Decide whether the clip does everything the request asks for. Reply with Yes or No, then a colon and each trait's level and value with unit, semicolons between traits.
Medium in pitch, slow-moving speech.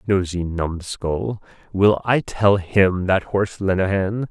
No: very low, 95 Hz; slow, 125 wpm